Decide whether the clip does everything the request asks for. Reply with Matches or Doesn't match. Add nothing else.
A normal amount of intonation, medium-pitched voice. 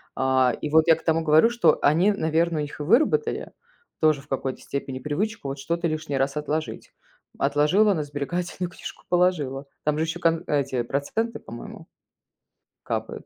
Matches